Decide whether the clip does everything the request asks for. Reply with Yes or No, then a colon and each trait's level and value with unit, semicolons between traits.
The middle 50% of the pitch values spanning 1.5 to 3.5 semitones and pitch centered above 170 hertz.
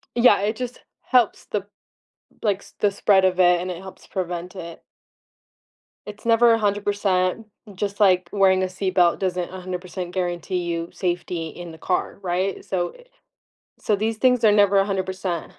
Yes: narrow, 2.4 semitones; high, 190 Hz